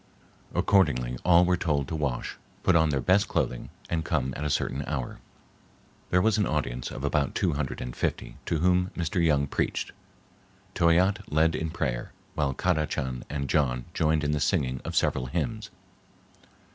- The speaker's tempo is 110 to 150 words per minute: No, average, 170 wpm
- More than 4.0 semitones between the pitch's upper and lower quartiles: Yes, average, 4.5 semitones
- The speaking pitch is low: Yes, very low, 75 Hz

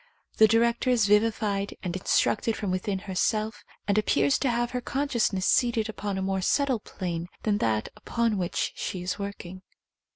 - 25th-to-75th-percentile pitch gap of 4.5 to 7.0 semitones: No, average, 3.5 semitones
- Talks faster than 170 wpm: No, average, 165 wpm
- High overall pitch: Yes, high, 210 Hz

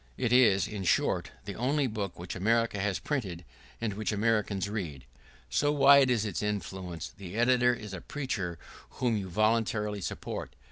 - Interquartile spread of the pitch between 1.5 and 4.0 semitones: Yes, average, 3.6 semitones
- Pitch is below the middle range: Yes, low, 105 Hz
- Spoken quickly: No, average, 160 wpm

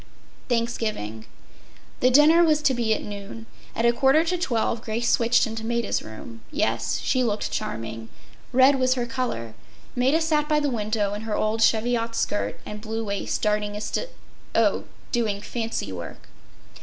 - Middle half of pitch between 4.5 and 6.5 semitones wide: No, average, 3.6 semitones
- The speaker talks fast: No, average, 170 wpm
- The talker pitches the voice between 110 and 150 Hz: No, high, 230 Hz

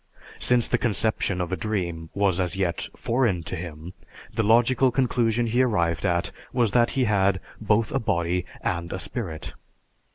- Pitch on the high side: No, low, 100 Hz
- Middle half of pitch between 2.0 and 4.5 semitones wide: No, average, 5.2 semitones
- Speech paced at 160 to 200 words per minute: Yes, average, 165 wpm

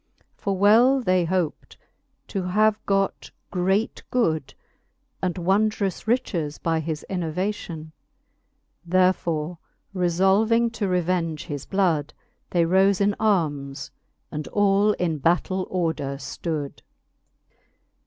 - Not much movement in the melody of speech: No, average, 3.7 semitones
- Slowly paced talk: Yes, slow, 105 wpm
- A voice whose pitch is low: No, medium, 185 Hz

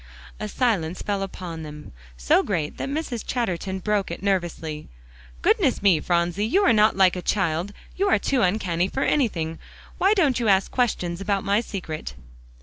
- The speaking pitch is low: No, high, 195 Hz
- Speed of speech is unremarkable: Yes, average, 170 wpm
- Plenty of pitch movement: No, average, 4.5 semitones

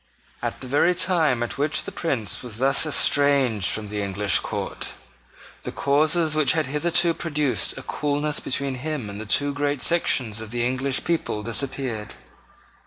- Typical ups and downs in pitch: Yes, average, 4.8 semitones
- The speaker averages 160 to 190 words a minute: Yes, average, 165 wpm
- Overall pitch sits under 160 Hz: Yes, medium, 140 Hz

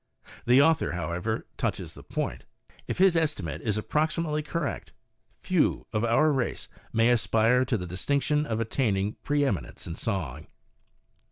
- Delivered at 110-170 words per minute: Yes, average, 140 wpm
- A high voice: No, low, 115 Hz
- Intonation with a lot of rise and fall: Yes, wide, 7.2 semitones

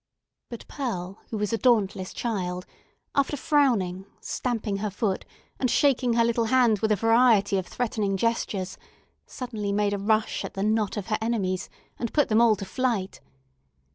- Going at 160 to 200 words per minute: Yes, average, 170 wpm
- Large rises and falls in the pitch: No, average, 3.3 semitones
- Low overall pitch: No, high, 215 Hz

